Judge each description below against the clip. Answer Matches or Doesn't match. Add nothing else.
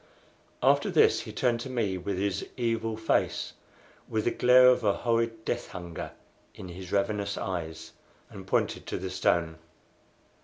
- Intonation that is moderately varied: Matches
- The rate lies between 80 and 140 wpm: Doesn't match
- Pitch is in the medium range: Doesn't match